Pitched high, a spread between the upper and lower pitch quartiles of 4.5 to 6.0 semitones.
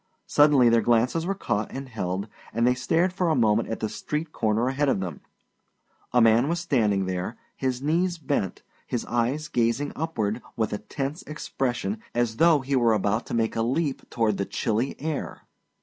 No: low, 125 Hz; average, 5.0 semitones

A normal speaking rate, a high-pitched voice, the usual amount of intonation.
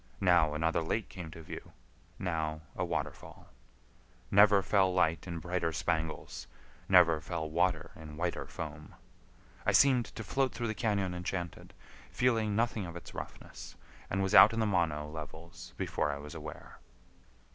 No: average, 155 wpm; very low, 85 Hz; average, 3.8 semitones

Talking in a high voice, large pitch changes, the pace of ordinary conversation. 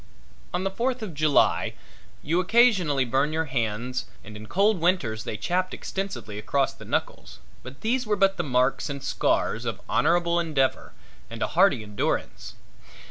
No: medium, 155 Hz; wide, 7.0 semitones; average, 160 wpm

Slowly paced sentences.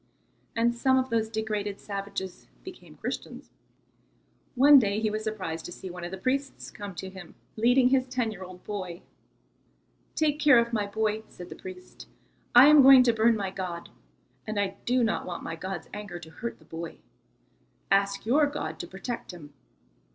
No: average, 180 wpm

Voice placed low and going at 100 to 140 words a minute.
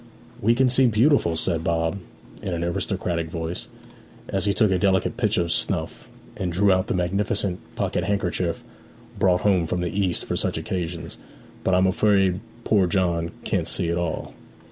No: very low, 90 Hz; average, 175 wpm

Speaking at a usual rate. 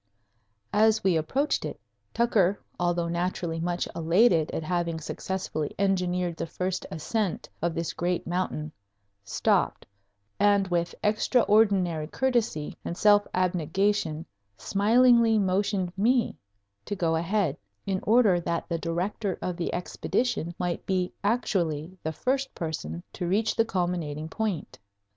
No: slow, 125 wpm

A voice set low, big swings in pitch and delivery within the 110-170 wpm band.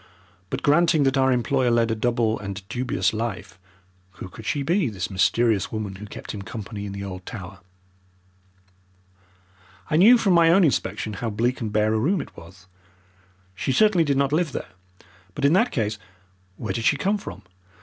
No: low, 115 Hz; wide, 6.0 semitones; average, 185 wpm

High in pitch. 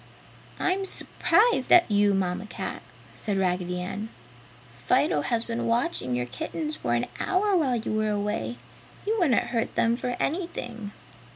Yes: high, 220 Hz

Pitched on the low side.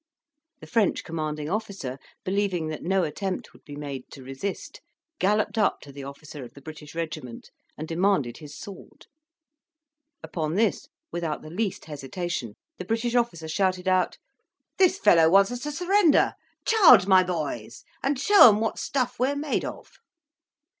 No: medium, 185 Hz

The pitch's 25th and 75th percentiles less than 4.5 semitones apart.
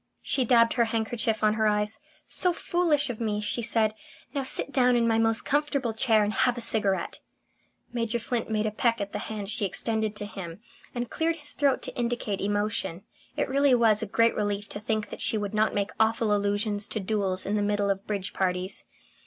Yes: narrow, 2.5 semitones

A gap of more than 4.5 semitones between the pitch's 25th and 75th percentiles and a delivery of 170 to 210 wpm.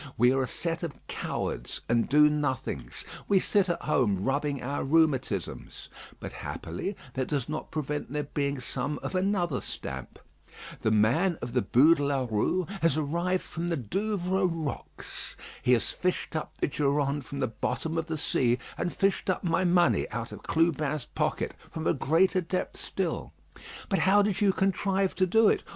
Yes: average, 5.2 semitones; average, 175 wpm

